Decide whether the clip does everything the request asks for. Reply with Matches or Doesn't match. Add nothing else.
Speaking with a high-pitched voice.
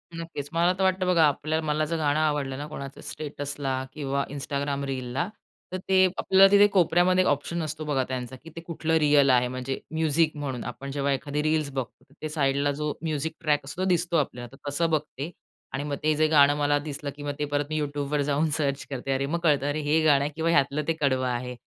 Doesn't match